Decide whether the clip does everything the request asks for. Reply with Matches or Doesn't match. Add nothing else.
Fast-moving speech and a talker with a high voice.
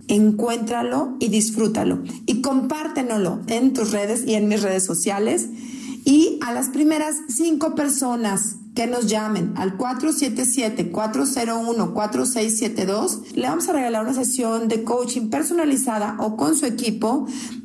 Doesn't match